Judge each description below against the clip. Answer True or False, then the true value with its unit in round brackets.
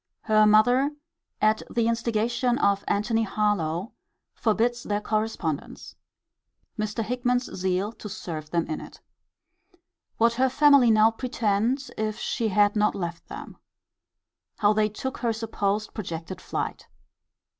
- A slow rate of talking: True (125 wpm)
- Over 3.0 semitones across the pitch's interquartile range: False (2.6 semitones)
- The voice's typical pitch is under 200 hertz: False (215 Hz)